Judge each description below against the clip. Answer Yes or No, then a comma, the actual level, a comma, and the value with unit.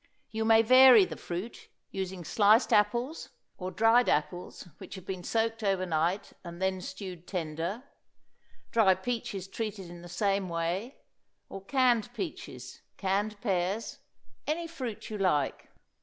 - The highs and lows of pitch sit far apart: No, average, 3.8 semitones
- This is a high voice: Yes, high, 195 Hz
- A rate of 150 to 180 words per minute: No, average, 140 wpm